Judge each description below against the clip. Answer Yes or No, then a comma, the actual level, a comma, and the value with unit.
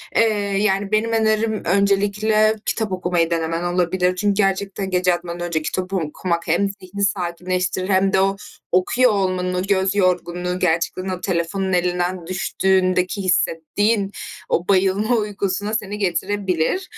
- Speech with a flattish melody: Yes, narrow, 2.1 semitones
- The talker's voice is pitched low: No, high, 190 Hz